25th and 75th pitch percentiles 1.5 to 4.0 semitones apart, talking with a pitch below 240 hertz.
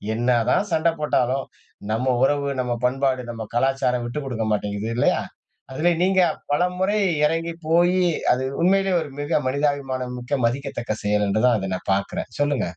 No: average, 4.5 semitones; low, 135 Hz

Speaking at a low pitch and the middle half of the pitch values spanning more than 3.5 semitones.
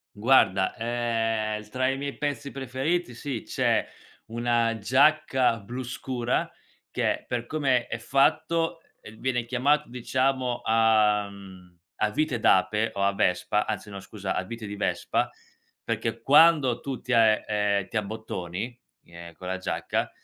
Yes: low, 115 Hz; average, 3.9 semitones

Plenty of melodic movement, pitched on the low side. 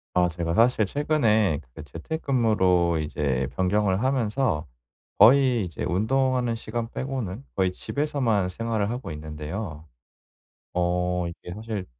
Yes: wide, 5.7 semitones; low, 105 Hz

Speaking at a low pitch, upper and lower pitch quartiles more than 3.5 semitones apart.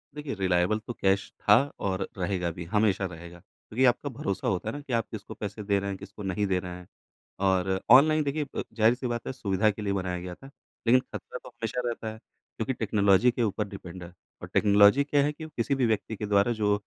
Yes: low, 105 Hz; average, 3.9 semitones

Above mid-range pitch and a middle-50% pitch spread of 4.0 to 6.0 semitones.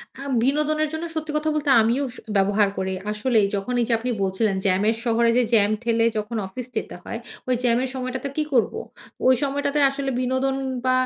Yes: very high, 250 Hz; average, 4.4 semitones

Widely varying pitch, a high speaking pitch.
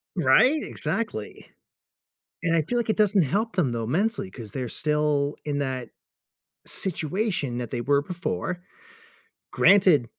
No: wide, 7.1 semitones; medium, 155 Hz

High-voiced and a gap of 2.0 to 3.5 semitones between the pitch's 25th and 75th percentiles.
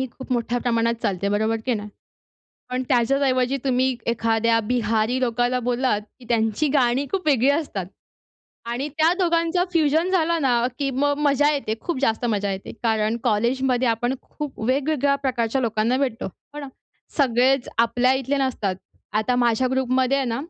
Yes: very high, 250 Hz; average, 3.2 semitones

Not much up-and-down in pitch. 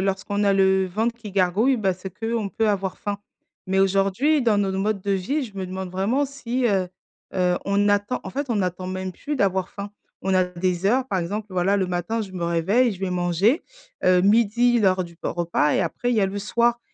No: average, 3.3 semitones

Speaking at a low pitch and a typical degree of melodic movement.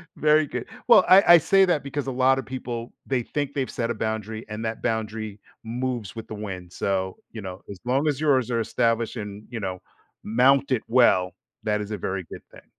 Yes: low, 115 Hz; average, 3.9 semitones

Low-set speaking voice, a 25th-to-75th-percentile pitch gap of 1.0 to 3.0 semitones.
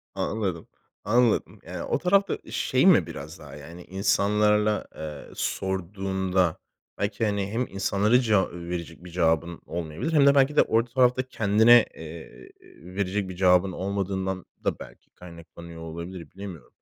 No: very low, 95 Hz; average, 3.6 semitones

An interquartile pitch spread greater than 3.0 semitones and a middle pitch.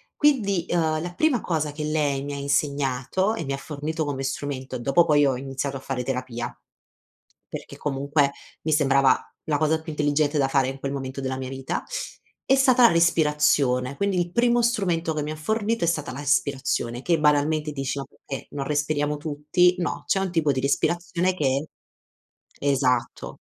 Yes: average, 3.6 semitones; medium, 150 Hz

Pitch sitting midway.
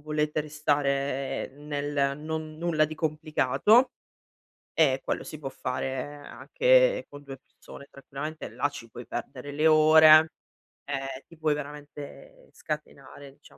Yes: medium, 150 Hz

